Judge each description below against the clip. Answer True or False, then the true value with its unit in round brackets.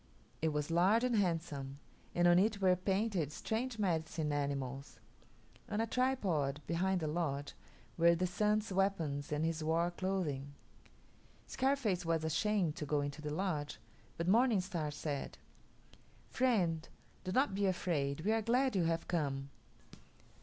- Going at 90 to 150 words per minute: True (145 wpm)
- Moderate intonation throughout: True (5.0 semitones)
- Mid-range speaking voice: True (175 Hz)